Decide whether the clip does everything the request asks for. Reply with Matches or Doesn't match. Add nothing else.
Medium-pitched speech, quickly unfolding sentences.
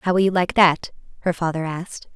Matches